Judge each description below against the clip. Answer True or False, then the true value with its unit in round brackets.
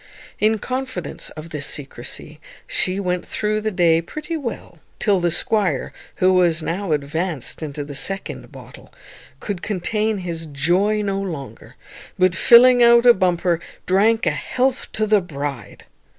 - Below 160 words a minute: True (150 wpm)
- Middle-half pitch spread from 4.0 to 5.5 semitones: True (4.8 semitones)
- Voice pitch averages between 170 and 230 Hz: True (185 Hz)